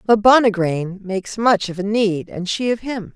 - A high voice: Yes, high, 205 Hz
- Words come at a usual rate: Yes, average, 170 wpm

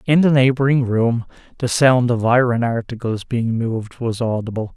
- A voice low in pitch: Yes, low, 120 Hz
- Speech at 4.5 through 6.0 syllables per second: Yes, 4.9 syllables/s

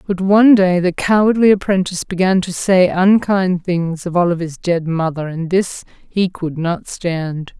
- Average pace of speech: Yes, average, 165 wpm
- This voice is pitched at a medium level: Yes, medium, 180 Hz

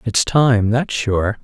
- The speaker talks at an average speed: Yes, average, 165 wpm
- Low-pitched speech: Yes, low, 115 Hz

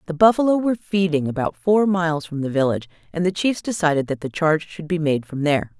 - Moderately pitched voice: Yes, medium, 165 Hz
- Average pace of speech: No, fast, 230 wpm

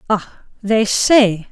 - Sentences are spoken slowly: Yes, slow, 120 wpm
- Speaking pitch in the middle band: No, high, 215 Hz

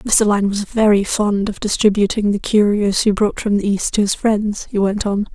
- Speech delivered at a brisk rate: Yes, fast, 225 wpm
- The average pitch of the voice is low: No, high, 205 Hz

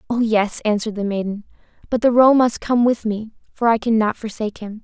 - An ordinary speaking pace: No, fast, 210 wpm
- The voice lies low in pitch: No, high, 220 Hz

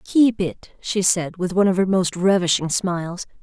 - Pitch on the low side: No, medium, 185 Hz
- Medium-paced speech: Yes, average, 195 wpm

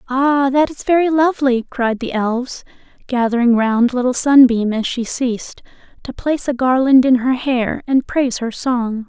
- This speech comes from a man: No, female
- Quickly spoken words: No, average, 170 wpm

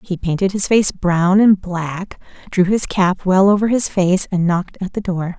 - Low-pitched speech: No, medium, 185 Hz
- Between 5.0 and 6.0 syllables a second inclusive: No, 4.5 syllables/s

